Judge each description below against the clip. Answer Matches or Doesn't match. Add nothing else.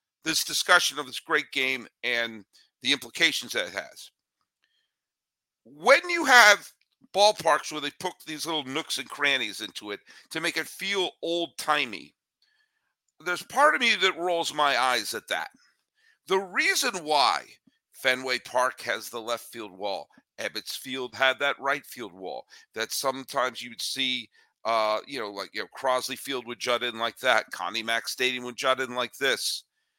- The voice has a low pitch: Doesn't match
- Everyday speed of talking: Matches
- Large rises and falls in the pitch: Matches